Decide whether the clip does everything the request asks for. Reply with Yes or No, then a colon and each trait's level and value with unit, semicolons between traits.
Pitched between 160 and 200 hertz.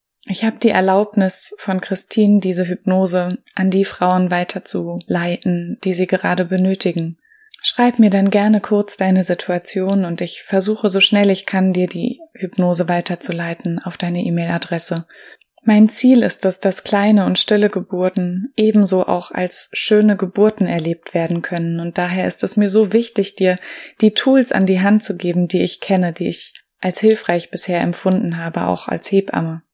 Yes: high, 190 Hz